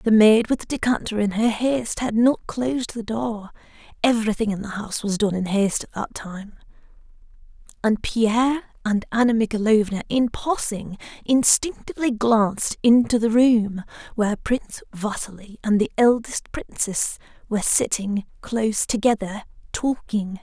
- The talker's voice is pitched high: Yes, high, 220 Hz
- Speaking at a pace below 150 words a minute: Yes, average, 140 wpm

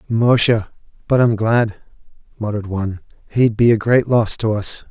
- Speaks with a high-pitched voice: No, low, 110 Hz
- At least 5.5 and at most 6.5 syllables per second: No, 5.1 syllables/s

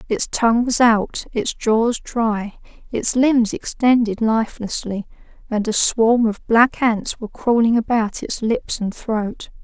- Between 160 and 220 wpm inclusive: No, average, 150 wpm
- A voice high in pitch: Yes, high, 225 Hz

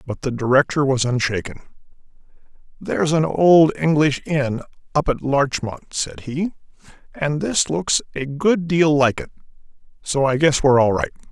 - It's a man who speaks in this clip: Yes, male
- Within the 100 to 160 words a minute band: Yes, average, 155 wpm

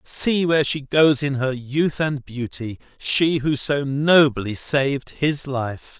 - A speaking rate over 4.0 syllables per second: No, 3.5 syllables/s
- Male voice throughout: Yes, male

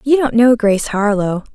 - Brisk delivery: No, average, 195 wpm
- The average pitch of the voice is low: No, high, 230 Hz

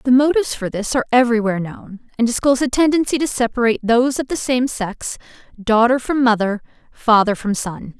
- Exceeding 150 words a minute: Yes, average, 180 wpm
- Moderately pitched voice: No, high, 240 Hz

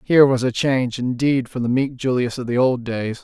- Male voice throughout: Yes, male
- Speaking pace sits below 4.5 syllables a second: No, 5.4 syllables/s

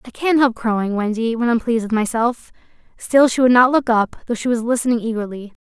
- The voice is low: No, high, 235 Hz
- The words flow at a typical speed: No, fast, 225 wpm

